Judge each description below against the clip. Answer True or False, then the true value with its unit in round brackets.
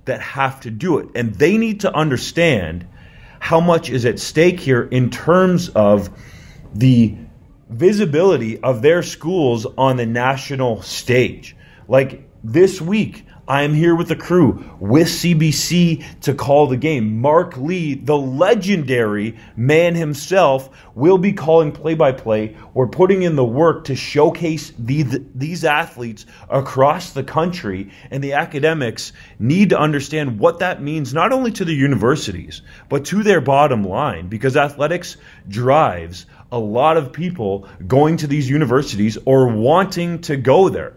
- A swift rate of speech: False (150 wpm)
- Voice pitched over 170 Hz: False (140 Hz)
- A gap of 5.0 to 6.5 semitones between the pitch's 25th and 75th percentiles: True (5.4 semitones)